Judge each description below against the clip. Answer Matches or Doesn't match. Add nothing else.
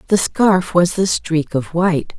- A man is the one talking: Doesn't match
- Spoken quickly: Doesn't match